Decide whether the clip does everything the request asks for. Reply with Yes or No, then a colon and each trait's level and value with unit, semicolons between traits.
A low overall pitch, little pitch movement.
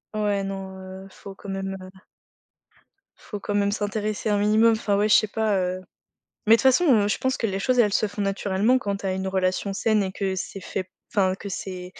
No: high, 200 Hz; narrow, 1.9 semitones